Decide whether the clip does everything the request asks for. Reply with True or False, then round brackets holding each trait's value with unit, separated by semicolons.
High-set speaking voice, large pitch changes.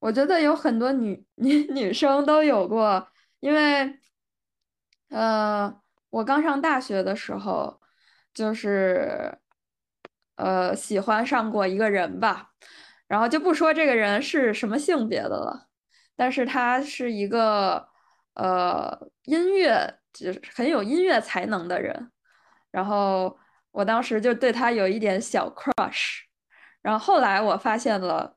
True (240 Hz; 6.0 semitones)